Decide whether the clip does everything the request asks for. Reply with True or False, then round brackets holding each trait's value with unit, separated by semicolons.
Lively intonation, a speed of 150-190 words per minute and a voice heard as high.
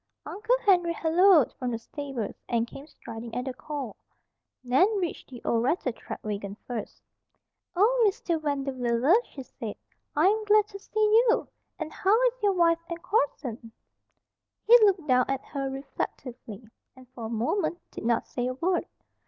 True (7.6 semitones; 160 wpm; 285 Hz)